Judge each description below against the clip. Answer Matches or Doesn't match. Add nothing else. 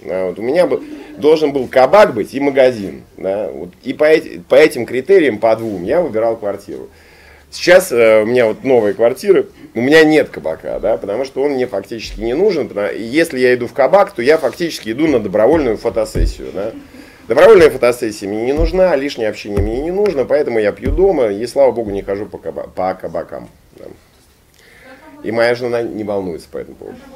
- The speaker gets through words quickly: Matches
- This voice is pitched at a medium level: Doesn't match